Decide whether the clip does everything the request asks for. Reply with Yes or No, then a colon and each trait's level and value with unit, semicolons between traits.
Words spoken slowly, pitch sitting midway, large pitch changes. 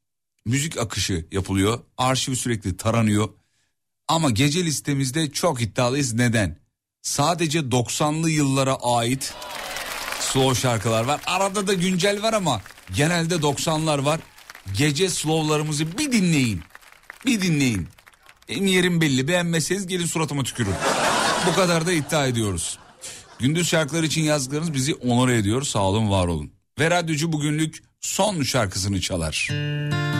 No: average, 125 wpm; medium, 145 Hz; wide, 5.8 semitones